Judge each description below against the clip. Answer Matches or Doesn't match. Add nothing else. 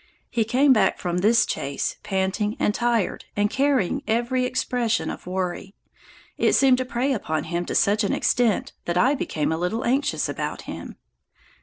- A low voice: Doesn't match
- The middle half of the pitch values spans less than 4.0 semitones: Doesn't match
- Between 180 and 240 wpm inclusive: Doesn't match